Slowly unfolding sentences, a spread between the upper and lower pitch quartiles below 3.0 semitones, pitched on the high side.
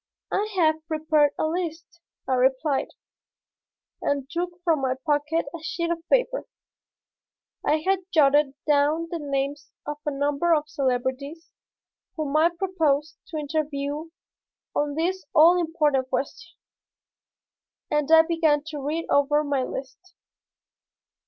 Yes: slow, 125 wpm; narrow, 2.6 semitones; very high, 305 Hz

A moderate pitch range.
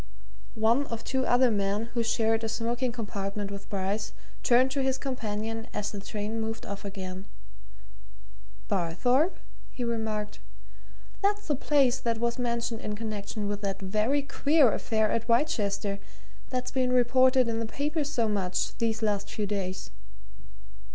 Yes: average, 3.4 semitones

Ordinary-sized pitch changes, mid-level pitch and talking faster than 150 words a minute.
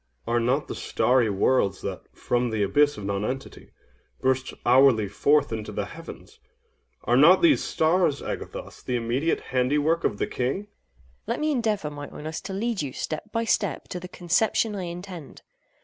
No: wide, 6.5 semitones; medium, 145 Hz; average, 170 wpm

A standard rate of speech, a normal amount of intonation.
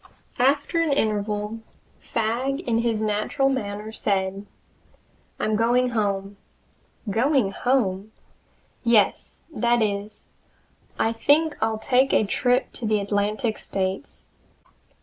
No: slow, 110 wpm; average, 3.5 semitones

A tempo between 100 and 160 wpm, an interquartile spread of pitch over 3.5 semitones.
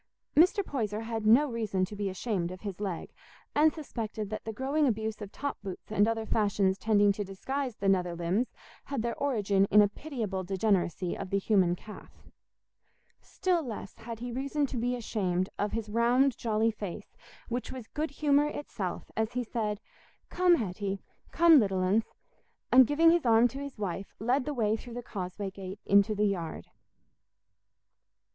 No: average, 175 wpm; average, 4.2 semitones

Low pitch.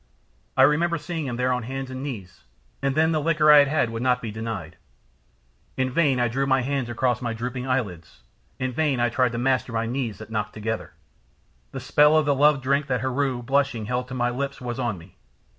Yes: low, 130 Hz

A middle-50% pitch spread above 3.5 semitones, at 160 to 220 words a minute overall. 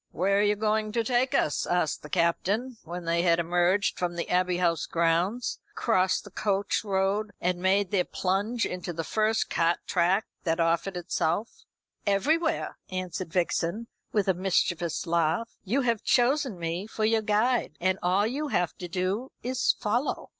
Yes: average, 3.9 semitones; average, 170 wpm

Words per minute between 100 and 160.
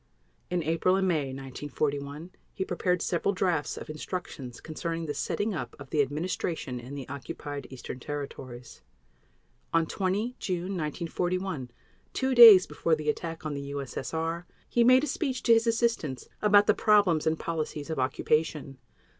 Yes: average, 155 wpm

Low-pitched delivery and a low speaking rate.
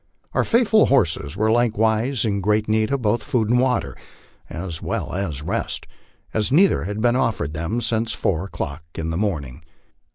No: low, 110 Hz; average, 170 wpm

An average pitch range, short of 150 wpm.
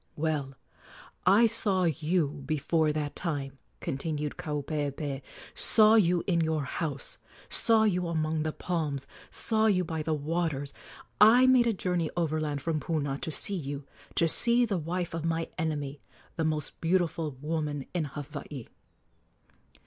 Yes: average, 3.4 semitones; average, 140 wpm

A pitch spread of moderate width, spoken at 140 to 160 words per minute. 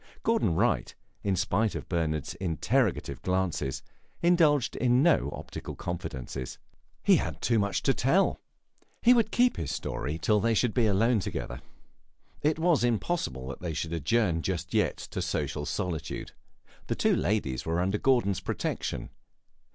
No: wide, 7.6 semitones; average, 150 wpm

